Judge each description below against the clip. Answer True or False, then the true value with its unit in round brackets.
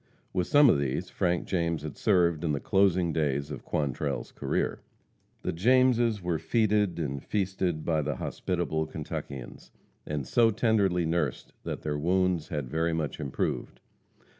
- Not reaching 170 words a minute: True (150 wpm)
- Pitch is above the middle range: False (85 Hz)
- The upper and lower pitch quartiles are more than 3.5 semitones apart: True (4.2 semitones)